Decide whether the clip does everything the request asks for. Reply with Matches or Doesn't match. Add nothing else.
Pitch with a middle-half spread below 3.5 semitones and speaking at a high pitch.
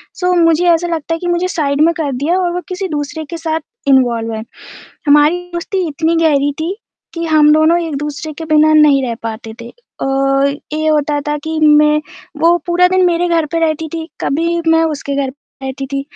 Matches